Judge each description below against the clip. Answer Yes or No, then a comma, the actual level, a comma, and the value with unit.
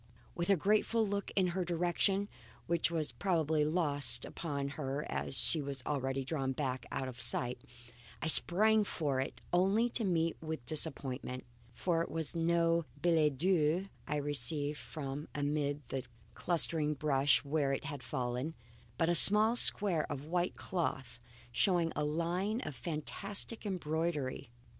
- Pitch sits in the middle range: Yes, medium, 155 Hz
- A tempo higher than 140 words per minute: Yes, average, 150 wpm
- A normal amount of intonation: Yes, average, 3.9 semitones